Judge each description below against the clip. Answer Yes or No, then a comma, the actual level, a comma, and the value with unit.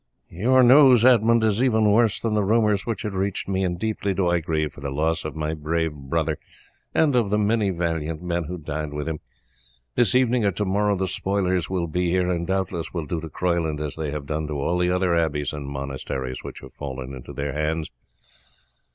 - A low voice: Yes, very low, 85 Hz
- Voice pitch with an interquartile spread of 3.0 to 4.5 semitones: No, average, 5.0 semitones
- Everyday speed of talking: No, fast, 215 wpm